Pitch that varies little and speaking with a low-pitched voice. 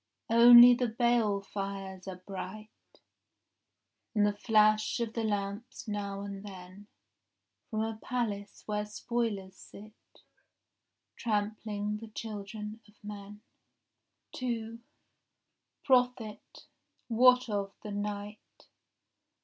No: narrow, 2.1 semitones; high, 210 Hz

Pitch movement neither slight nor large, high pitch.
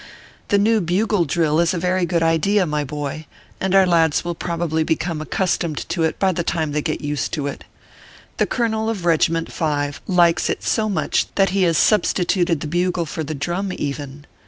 No: average, 3.2 semitones; medium, 170 Hz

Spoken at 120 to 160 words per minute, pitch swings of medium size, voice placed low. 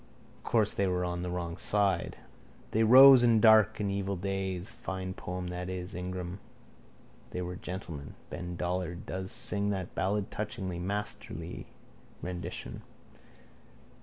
No: slow, 135 wpm; narrow, 2.3 semitones; very low, 95 Hz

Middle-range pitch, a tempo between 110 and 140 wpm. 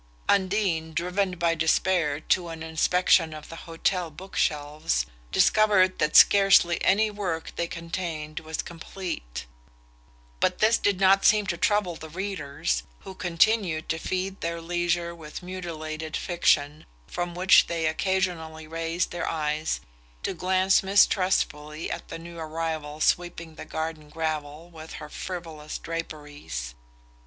Yes: medium, 165 Hz; slow, 135 wpm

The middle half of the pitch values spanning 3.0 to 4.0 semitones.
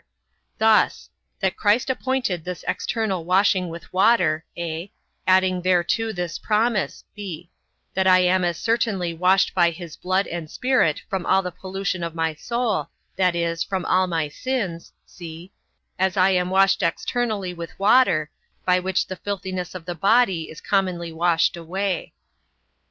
No: narrow, 2.6 semitones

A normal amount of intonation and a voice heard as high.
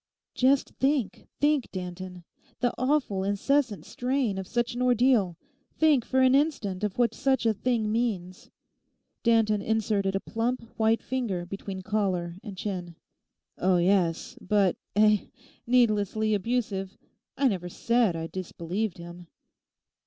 Yes: average, 4.7 semitones; high, 215 Hz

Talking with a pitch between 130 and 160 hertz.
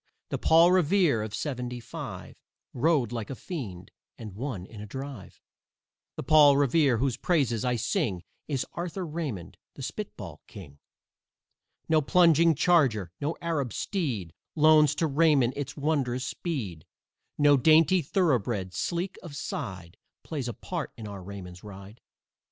Yes: medium, 140 Hz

